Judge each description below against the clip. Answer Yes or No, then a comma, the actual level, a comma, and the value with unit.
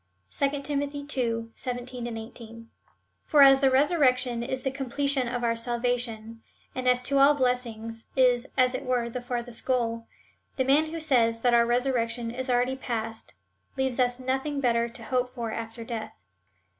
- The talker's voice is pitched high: Yes, very high, 250 Hz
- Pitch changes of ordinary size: No, narrow, 2.2 semitones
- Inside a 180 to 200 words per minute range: No, average, 165 wpm